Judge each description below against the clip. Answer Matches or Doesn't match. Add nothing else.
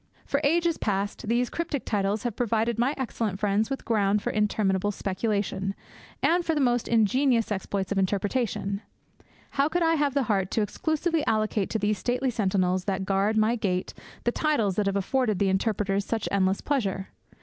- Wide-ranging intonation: Doesn't match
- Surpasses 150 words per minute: Matches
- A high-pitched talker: Matches